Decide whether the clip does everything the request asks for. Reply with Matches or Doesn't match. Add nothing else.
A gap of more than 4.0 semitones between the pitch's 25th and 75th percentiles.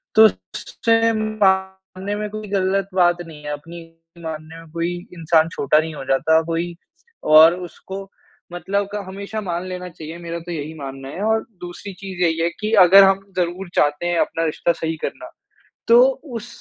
Doesn't match